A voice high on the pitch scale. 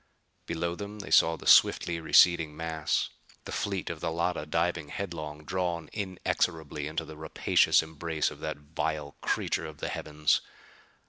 No: very low, 80 Hz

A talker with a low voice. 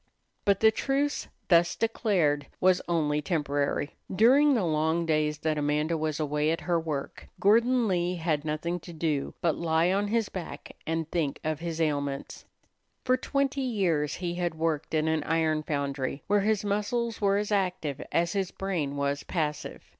No: medium, 165 Hz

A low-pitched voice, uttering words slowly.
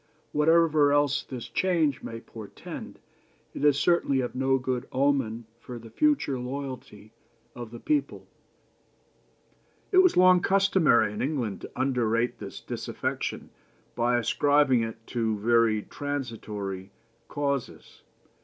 Yes: low, 130 Hz; slow, 120 wpm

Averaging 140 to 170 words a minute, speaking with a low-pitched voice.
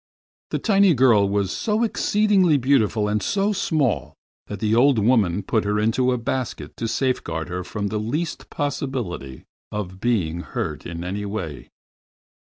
Yes: average, 155 wpm; low, 110 Hz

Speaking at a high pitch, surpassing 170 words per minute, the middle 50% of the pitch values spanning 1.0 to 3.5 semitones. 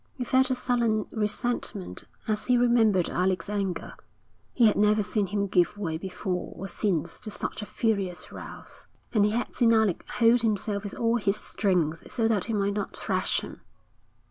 Yes: high, 210 Hz; average, 180 wpm; average, 2.8 semitones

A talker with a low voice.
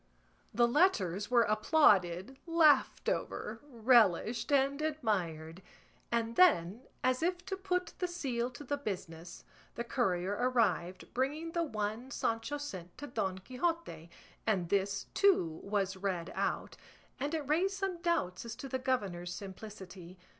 No: high, 235 Hz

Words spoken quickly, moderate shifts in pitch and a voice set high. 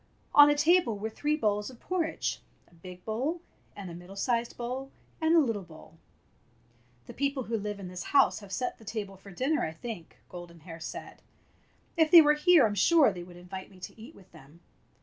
No: fast, 210 wpm; wide, 7.7 semitones; high, 220 Hz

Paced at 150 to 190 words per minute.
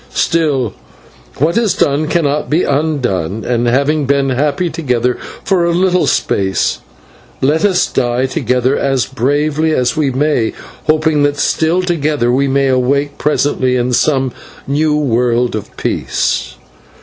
No: slow, 135 wpm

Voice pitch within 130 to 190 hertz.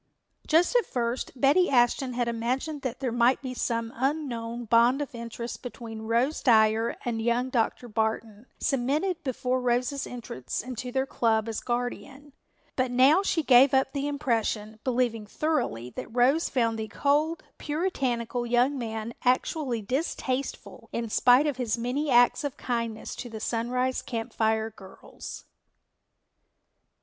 No: high, 245 Hz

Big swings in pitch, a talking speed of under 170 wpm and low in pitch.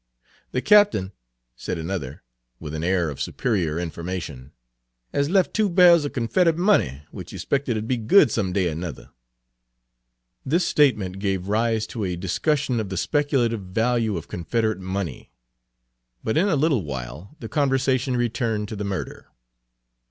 Yes: wide, 7.1 semitones; average, 155 wpm; low, 110 Hz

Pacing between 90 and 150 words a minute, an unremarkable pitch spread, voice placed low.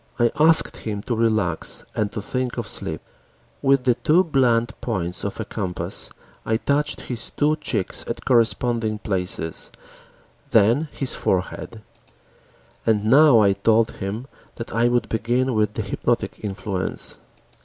Yes: average, 145 wpm; average, 3.6 semitones; low, 115 Hz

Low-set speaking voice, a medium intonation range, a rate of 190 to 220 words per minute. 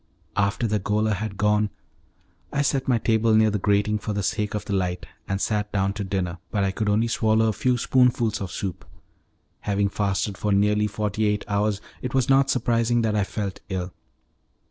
No: low, 105 Hz; narrow, 1.9 semitones; average, 195 wpm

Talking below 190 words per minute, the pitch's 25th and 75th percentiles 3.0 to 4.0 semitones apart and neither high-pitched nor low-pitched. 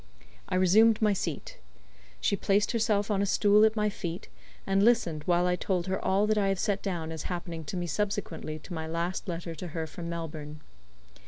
No: average, 200 wpm; average, 3.7 semitones; medium, 180 Hz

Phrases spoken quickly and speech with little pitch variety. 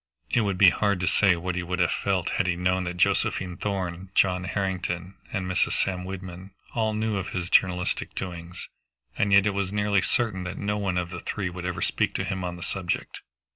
Yes: fast, 215 wpm; narrow, 1.8 semitones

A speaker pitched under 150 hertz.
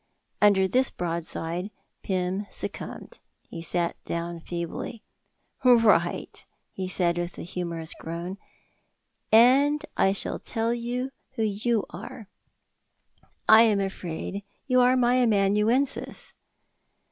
No: high, 200 Hz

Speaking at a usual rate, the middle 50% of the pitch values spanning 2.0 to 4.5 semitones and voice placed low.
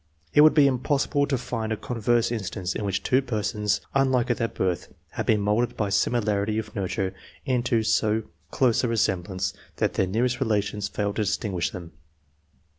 Yes: average, 180 wpm; average, 3.3 semitones; low, 110 Hz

